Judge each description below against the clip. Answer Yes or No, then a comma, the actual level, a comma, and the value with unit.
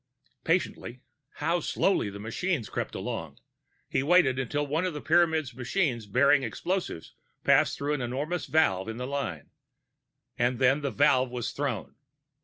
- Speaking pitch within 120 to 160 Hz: Yes, low, 135 Hz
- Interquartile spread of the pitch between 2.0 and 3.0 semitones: No, average, 4.6 semitones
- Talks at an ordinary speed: Yes, average, 150 wpm